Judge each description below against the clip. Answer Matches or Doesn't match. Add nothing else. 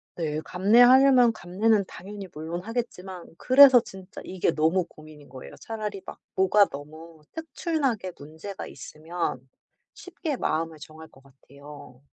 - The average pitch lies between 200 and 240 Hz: Doesn't match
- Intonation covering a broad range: Matches